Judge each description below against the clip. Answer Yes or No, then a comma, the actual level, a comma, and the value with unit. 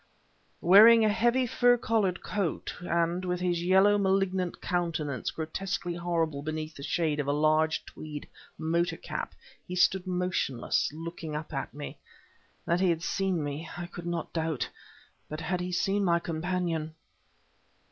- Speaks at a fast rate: No, average, 150 wpm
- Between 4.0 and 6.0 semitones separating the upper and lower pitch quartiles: No, average, 2.8 semitones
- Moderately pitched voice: Yes, medium, 175 Hz